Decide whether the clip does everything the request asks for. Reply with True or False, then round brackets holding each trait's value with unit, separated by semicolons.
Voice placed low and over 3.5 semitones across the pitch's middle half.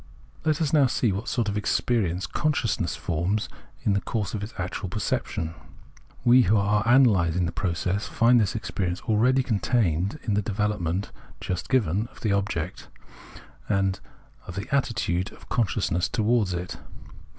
True (105 Hz; 4.3 semitones)